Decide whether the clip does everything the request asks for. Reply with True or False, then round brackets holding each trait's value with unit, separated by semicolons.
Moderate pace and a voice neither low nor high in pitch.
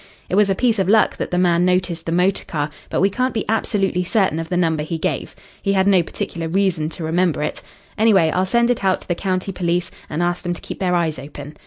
False (250 wpm; 180 Hz)